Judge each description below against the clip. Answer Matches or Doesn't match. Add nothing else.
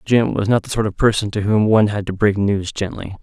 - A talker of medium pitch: Doesn't match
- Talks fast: Matches